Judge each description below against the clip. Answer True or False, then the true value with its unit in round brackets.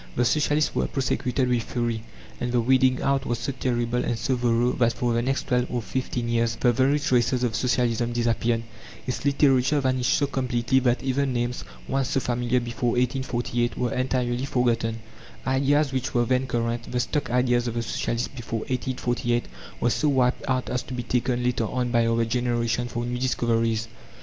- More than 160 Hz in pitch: False (125 Hz)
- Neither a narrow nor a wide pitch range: False (1.5 semitones)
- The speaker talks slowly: False (185 wpm)